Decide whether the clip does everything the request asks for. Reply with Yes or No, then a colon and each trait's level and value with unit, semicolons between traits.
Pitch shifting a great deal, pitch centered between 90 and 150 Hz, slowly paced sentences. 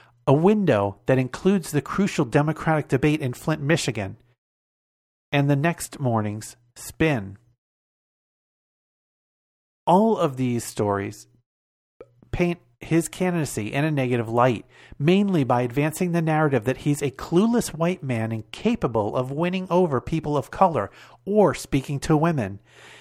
Yes: wide, 5.8 semitones; medium, 140 Hz; slow, 130 wpm